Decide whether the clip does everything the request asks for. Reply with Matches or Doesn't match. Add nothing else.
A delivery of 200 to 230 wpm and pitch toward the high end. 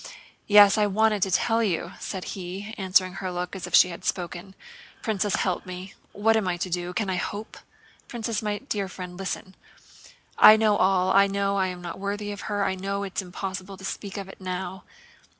Matches